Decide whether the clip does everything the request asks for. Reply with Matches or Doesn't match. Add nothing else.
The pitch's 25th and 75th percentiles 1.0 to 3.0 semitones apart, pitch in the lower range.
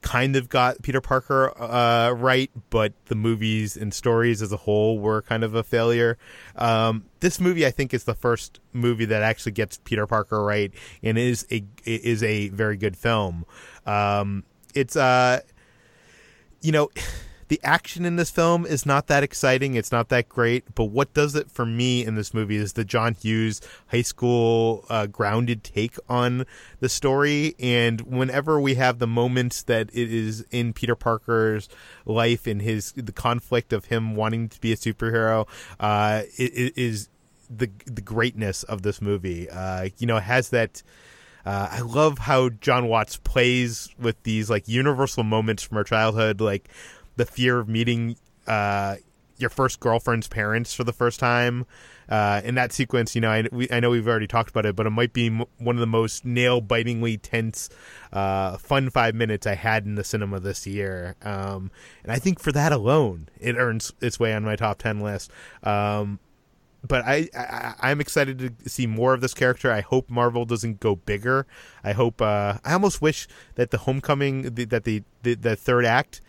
Matches